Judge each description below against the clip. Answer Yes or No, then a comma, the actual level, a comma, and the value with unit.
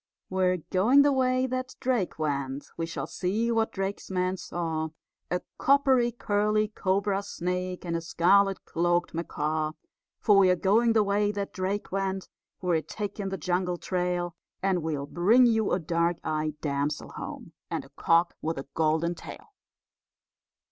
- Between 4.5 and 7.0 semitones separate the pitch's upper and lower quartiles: No, average, 3.6 semitones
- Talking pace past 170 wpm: No, average, 155 wpm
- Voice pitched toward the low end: No, medium, 185 Hz